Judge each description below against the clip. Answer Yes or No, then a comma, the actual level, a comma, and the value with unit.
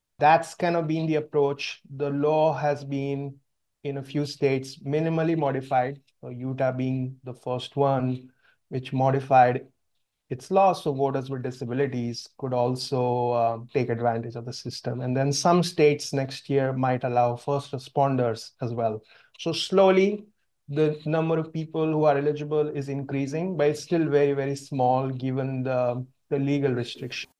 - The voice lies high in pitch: No, medium, 140 Hz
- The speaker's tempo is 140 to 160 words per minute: Yes, average, 155 wpm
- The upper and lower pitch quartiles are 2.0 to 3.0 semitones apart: Yes, average, 2.7 semitones